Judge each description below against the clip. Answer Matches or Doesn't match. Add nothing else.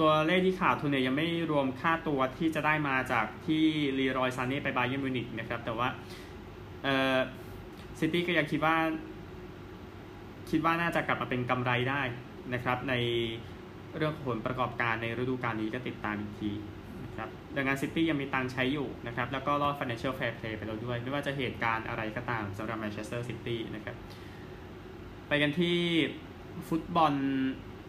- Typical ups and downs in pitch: Matches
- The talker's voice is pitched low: Matches